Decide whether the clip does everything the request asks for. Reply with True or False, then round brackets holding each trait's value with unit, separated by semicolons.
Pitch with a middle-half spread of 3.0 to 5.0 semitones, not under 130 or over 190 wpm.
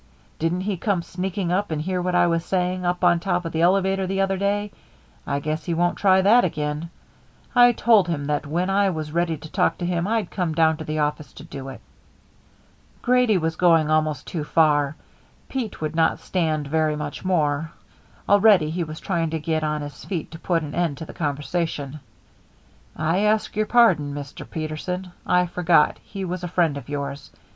False (3.3 semitones; 200 wpm)